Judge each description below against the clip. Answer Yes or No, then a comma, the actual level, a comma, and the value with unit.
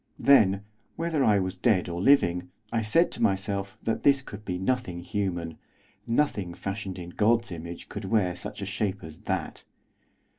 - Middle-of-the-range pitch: No, low, 100 Hz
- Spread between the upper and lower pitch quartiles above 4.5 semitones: No, average, 4.0 semitones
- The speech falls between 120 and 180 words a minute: Yes, average, 165 wpm